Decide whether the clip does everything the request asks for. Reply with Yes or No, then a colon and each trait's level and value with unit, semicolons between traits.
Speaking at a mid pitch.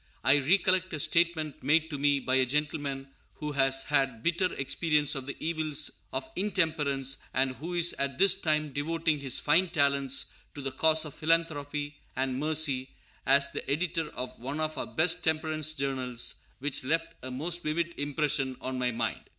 Yes: medium, 145 Hz